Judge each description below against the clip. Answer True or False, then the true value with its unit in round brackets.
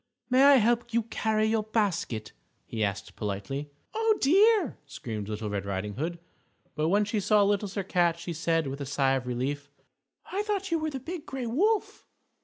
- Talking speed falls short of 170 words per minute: False (190 wpm)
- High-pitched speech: True (200 Hz)